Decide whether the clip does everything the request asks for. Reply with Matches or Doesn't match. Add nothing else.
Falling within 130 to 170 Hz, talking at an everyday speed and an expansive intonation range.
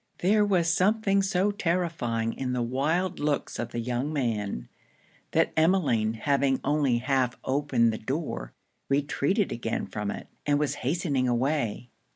Matches